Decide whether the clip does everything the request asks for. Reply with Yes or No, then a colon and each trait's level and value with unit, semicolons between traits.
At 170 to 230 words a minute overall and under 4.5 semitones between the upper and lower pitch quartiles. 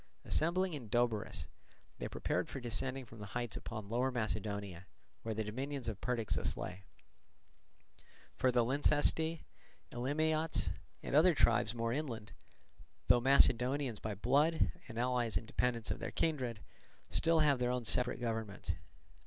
No: average, 140 wpm; average, 3.8 semitones